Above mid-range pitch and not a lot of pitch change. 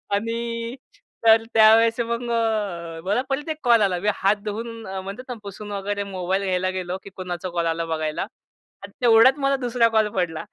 No: high, 210 Hz; average, 3.7 semitones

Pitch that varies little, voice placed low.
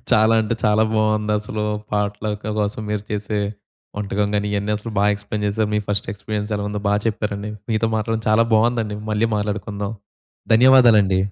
Yes: narrow, 0.9 semitones; low, 105 Hz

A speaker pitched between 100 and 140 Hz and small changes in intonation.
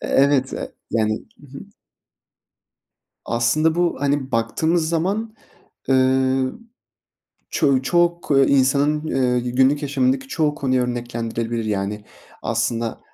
No: low, 135 Hz; average, 4.0 semitones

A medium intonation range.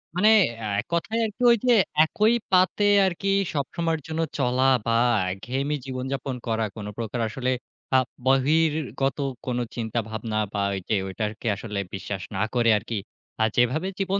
No: wide, 6.2 semitones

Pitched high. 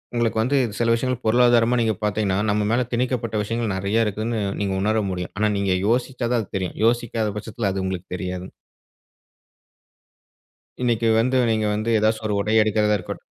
No: low, 110 Hz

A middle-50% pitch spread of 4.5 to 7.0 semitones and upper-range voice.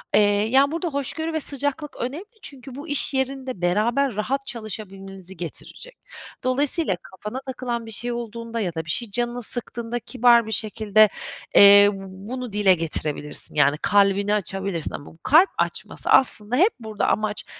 Yes: average, 4.9 semitones; high, 230 Hz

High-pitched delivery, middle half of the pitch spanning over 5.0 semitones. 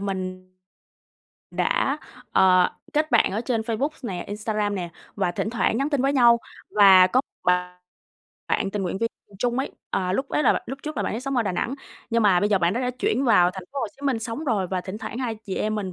No: high, 215 Hz; average, 4.7 semitones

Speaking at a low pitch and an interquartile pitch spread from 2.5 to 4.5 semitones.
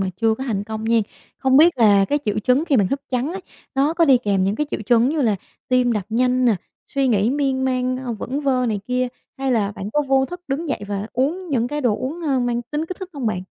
No: very high, 255 Hz; average, 4.0 semitones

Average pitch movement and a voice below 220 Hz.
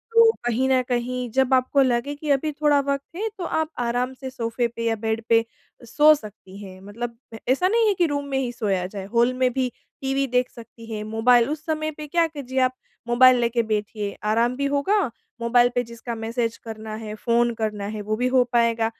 No: average, 3.3 semitones; high, 245 Hz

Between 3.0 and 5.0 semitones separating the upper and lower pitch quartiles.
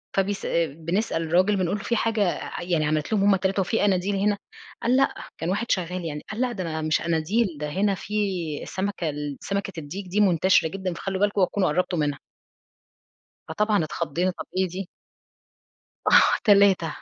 Yes: average, 3.6 semitones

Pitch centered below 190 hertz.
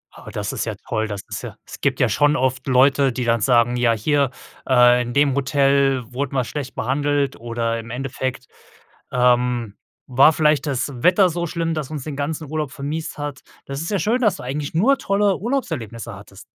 Yes: low, 135 Hz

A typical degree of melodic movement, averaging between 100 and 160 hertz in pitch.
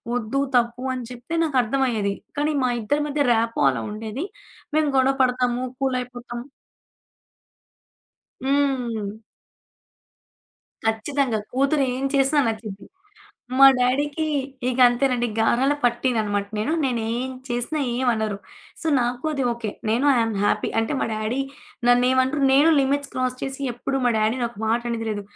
No: average, 3.0 semitones; very high, 250 Hz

